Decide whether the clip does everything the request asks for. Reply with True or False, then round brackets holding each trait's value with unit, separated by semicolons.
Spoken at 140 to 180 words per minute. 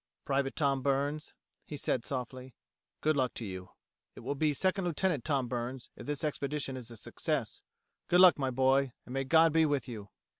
False (190 wpm)